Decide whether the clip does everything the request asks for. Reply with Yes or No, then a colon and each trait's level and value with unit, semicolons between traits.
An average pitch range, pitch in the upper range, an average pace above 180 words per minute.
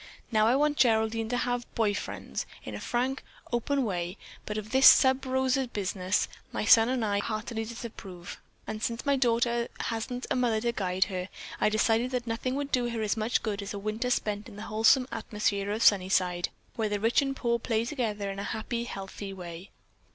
Yes: average, 3.0 semitones; high, 225 Hz; average, 200 wpm